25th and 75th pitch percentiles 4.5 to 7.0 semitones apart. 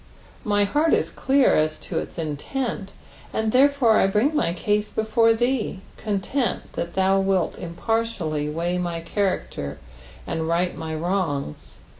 Yes: average, 5.2 semitones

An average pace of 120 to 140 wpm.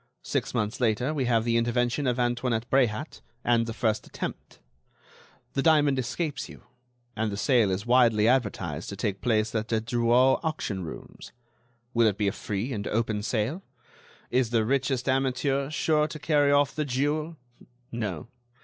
No: average, 165 wpm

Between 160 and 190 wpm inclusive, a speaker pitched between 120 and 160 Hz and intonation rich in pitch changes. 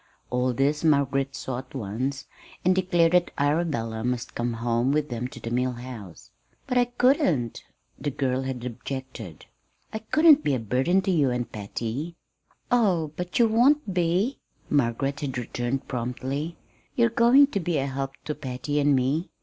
Yes: average, 165 wpm; medium, 140 Hz; wide, 5.8 semitones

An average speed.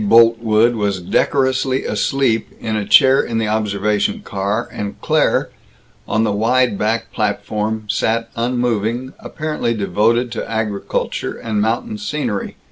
No: slow, 125 wpm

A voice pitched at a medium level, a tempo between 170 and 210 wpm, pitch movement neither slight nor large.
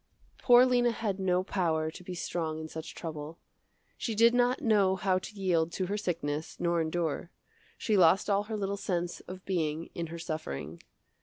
Yes: medium, 180 Hz; average, 180 wpm; average, 4.0 semitones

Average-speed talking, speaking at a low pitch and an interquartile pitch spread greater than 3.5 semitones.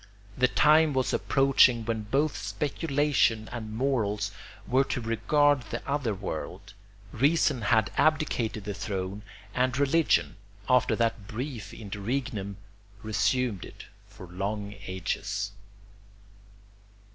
No: slow, 110 wpm; low, 115 Hz; average, 4.7 semitones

